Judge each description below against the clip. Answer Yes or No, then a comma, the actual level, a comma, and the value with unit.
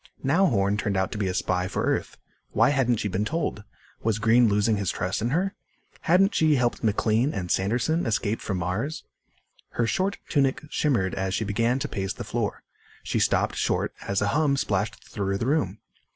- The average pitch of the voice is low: Yes, low, 110 Hz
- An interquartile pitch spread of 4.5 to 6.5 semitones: Yes, wide, 5.5 semitones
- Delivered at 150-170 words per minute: No, average, 195 wpm